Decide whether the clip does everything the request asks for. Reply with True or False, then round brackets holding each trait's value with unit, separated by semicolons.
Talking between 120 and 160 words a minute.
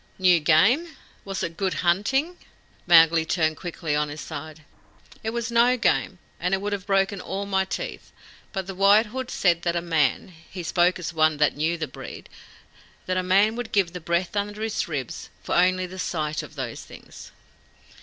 False (185 wpm)